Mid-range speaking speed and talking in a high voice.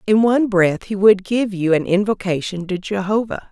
Yes: average, 190 wpm; high, 200 Hz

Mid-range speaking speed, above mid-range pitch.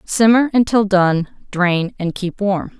Yes: average, 150 wpm; high, 195 Hz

